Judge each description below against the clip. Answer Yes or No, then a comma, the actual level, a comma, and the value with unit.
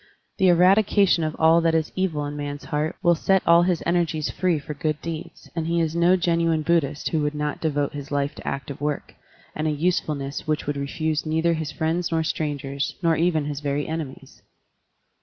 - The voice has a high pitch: No, medium, 155 Hz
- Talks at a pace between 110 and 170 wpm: No, average, 195 wpm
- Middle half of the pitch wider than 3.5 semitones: No, narrow, 2.4 semitones